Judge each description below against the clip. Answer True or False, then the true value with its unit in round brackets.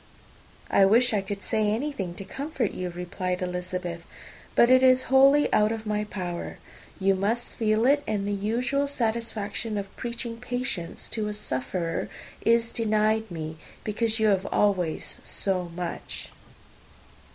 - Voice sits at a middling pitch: False (210 Hz)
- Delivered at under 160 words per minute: True (145 wpm)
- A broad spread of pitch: False (4.1 semitones)